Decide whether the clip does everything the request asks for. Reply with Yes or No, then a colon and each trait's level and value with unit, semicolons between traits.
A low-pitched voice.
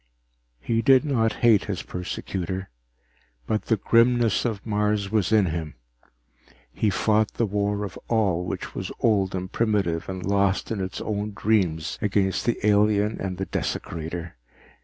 Yes: low, 100 Hz